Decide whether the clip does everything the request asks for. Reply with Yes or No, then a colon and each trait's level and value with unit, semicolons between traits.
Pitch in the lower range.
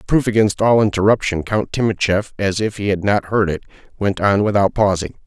Yes: low, 100 Hz